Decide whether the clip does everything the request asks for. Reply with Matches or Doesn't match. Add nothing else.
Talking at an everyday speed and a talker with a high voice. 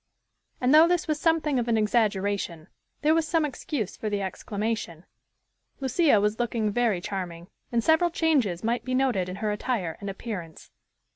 Matches